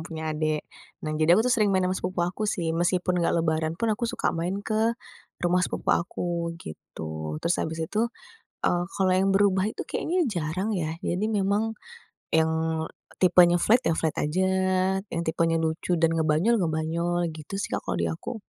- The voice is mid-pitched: Yes, medium, 175 Hz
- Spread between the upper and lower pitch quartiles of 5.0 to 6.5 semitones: No, average, 3.3 semitones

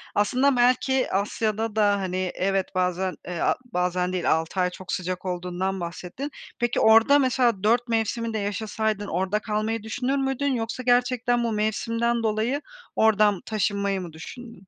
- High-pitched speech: Yes, high, 215 Hz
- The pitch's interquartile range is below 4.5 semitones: Yes, average, 4.1 semitones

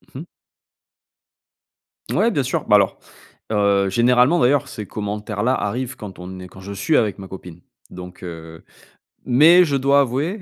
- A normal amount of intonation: No, wide, 5.9 semitones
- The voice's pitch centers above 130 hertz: No, low, 105 Hz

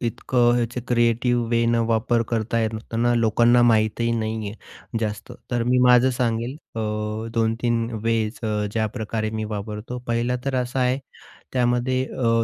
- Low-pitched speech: Yes, low, 115 Hz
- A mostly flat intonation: Yes, narrow, 1.5 semitones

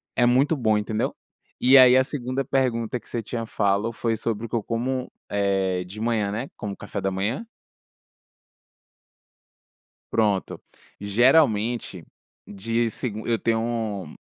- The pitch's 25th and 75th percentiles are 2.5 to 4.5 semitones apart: Yes, average, 3.1 semitones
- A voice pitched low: Yes, low, 115 Hz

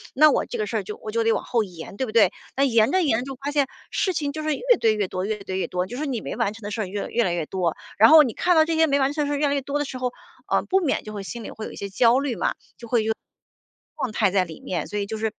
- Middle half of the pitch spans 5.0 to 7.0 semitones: Yes, wide, 5.4 semitones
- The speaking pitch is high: Yes, high, 230 Hz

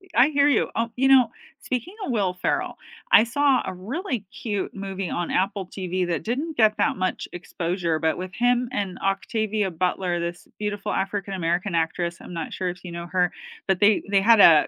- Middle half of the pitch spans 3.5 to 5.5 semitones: Yes, average, 4.3 semitones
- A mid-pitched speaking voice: No, high, 195 Hz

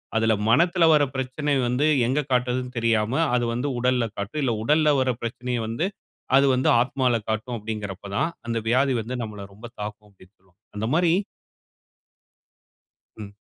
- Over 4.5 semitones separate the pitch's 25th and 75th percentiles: No, average, 3.6 semitones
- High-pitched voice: No, low, 125 Hz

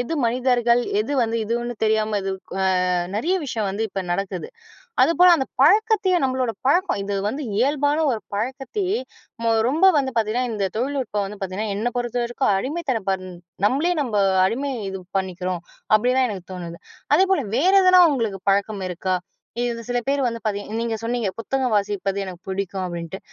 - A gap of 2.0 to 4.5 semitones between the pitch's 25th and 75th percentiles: No, average, 5.3 semitones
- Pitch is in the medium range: No, high, 230 Hz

